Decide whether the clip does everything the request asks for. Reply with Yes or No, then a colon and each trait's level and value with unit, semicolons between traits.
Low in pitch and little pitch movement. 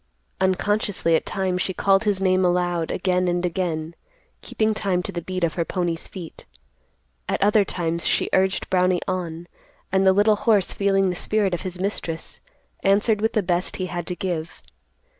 No: medium, 185 Hz; narrow, 2.0 semitones